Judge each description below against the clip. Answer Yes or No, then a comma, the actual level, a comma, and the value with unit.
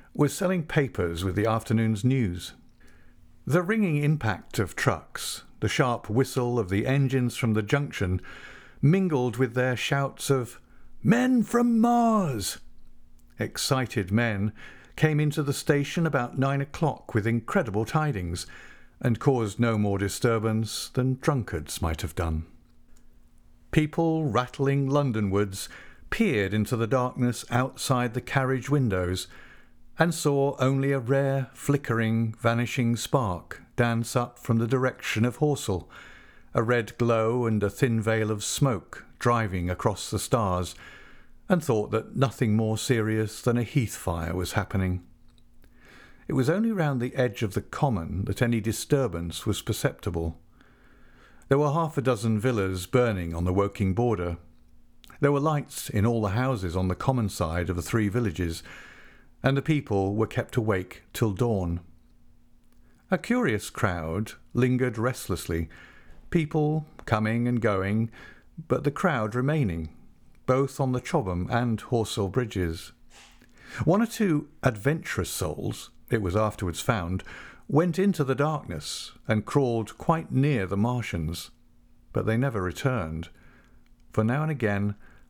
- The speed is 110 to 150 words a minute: Yes, average, 140 wpm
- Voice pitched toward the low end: Yes, low, 120 Hz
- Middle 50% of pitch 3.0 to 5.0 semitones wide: No, wide, 5.4 semitones